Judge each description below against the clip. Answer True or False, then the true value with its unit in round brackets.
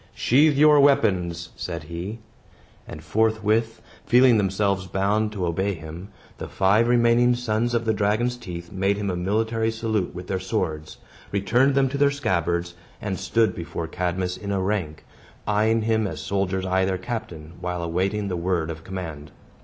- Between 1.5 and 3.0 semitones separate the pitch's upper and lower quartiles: False (4.0 semitones)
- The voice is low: True (100 Hz)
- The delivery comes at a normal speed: True (165 wpm)